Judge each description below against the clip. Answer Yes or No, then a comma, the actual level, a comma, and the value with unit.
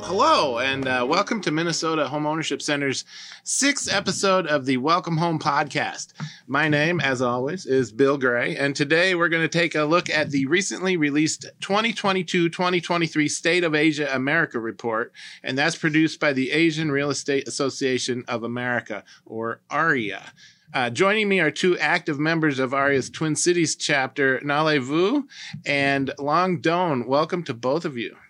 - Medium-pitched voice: Yes, medium, 150 Hz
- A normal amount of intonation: Yes, average, 3.8 semitones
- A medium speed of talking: Yes, average, 165 wpm